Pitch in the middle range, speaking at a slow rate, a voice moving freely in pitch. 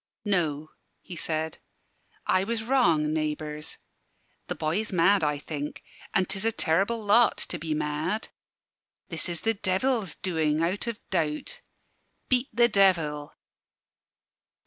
No: medium, 170 Hz; slow, 130 wpm; average, 5.0 semitones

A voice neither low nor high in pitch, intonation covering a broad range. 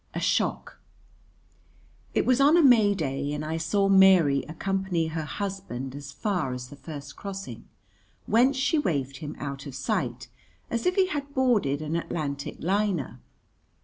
Yes: medium, 165 Hz; wide, 6.7 semitones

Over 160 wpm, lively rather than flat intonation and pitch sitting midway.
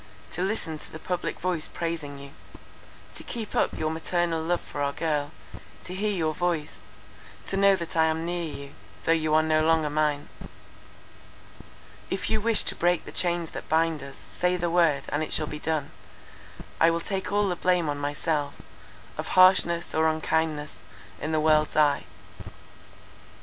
No: average, 170 wpm; narrow, 2.4 semitones; medium, 160 Hz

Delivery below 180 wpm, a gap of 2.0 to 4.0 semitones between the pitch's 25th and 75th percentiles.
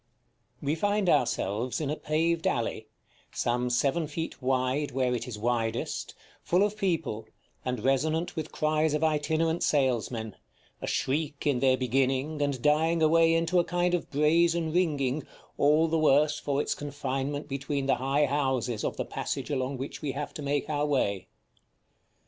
Yes: average, 165 wpm; average, 3.5 semitones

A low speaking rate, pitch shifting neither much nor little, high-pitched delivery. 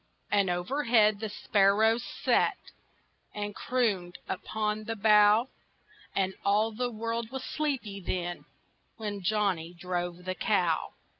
Yes: slow, 120 wpm; average, 3.3 semitones; high, 210 Hz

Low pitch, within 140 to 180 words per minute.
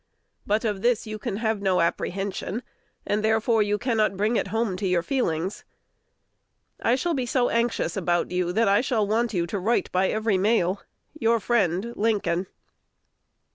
No: high, 215 Hz; average, 165 wpm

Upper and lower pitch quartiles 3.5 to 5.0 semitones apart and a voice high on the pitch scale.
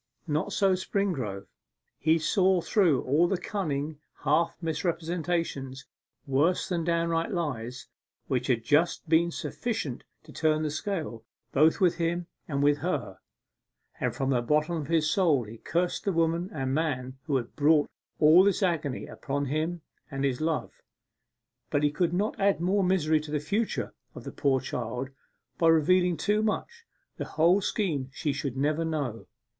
No: average, 3.9 semitones; medium, 160 Hz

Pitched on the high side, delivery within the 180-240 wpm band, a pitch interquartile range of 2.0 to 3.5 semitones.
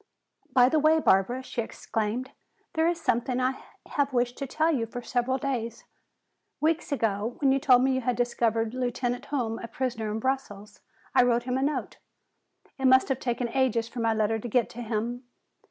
Yes: high, 245 Hz; average, 190 wpm; narrow, 2.5 semitones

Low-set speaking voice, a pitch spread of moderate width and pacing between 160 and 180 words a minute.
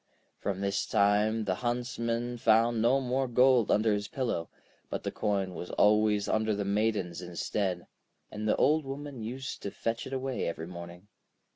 Yes: low, 110 Hz; average, 3.3 semitones; average, 165 wpm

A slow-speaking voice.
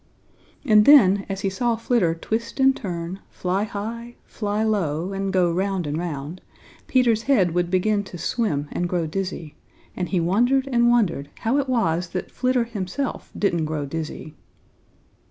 No: average, 160 wpm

